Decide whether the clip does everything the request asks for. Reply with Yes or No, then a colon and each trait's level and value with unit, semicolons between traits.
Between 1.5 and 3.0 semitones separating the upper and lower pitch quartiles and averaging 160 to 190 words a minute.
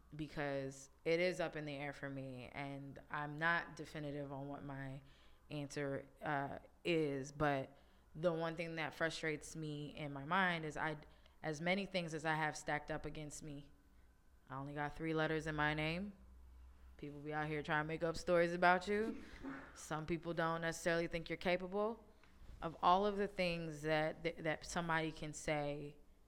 Yes: narrow, 2.6 semitones; average, 180 wpm